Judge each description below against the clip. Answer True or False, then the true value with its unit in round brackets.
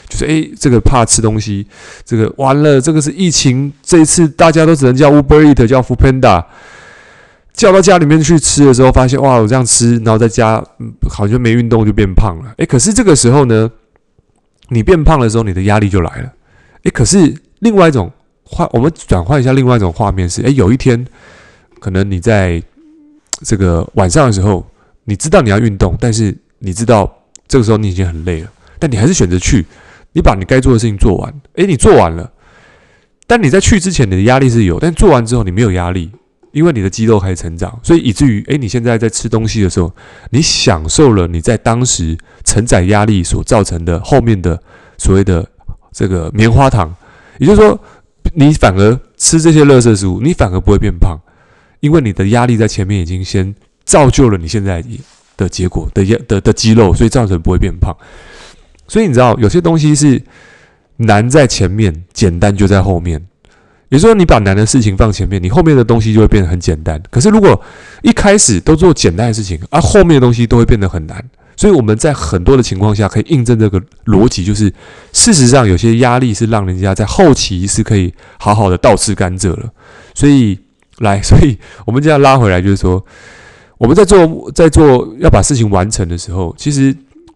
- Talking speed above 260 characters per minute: True (315 characters per minute)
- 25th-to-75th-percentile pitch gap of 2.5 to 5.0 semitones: False (5.4 semitones)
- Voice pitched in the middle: False (115 Hz)